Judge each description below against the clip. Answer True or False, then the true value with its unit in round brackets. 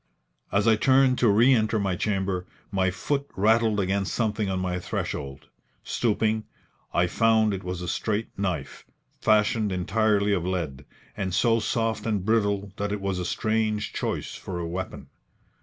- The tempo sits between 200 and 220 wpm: False (160 wpm)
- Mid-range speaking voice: False (100 Hz)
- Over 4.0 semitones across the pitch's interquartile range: False (3.0 semitones)